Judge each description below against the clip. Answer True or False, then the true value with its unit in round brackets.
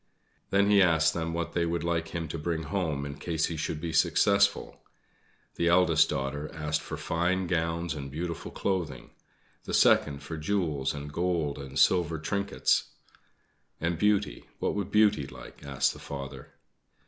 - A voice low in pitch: True (85 Hz)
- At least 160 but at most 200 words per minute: True (165 wpm)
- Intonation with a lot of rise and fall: False (3.2 semitones)